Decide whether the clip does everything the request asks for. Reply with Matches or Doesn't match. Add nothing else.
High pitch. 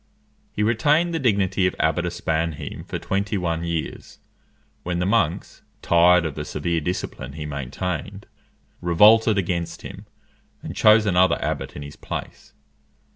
Doesn't match